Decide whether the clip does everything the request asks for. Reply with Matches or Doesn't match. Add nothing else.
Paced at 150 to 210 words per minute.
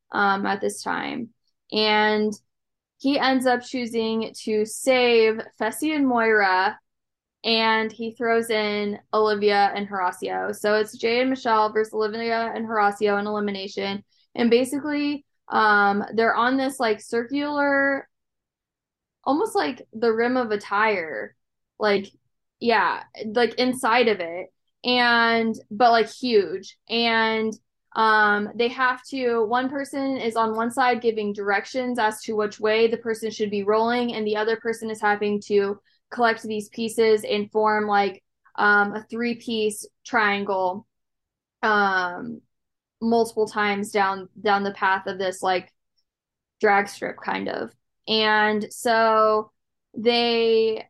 Doesn't match